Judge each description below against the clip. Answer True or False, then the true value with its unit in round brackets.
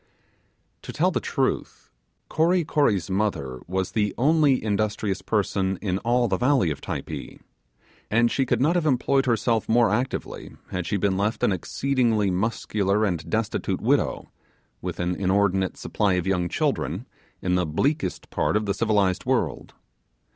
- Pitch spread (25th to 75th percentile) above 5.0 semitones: False (4.3 semitones)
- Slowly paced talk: False (155 wpm)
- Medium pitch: False (105 Hz)